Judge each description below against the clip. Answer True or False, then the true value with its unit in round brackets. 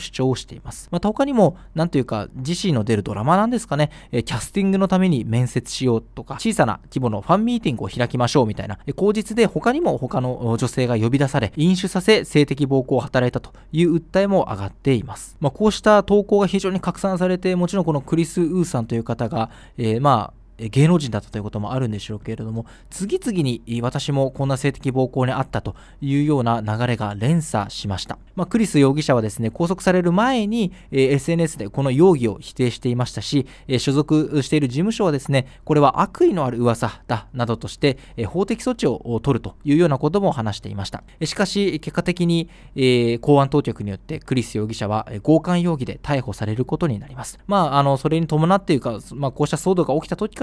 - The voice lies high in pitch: False (140 Hz)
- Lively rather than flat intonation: True (6.7 semitones)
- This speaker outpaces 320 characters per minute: True (430 characters per minute)